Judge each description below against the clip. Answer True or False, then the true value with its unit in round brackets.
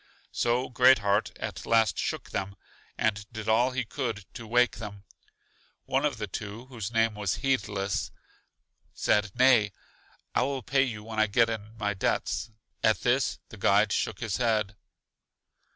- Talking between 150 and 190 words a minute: True (160 wpm)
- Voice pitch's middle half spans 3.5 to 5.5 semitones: False (2.9 semitones)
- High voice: False (110 Hz)